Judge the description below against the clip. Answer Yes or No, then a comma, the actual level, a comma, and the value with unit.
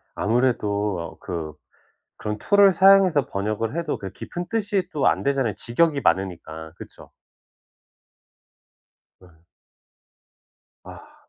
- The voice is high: No, low, 115 Hz